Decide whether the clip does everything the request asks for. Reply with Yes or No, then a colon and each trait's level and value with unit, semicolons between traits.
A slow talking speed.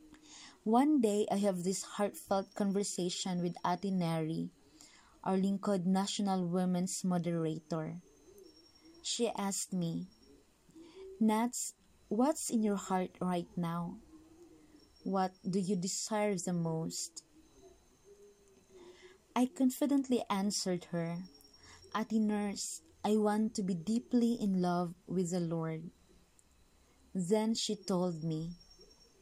Yes: slow, 105 wpm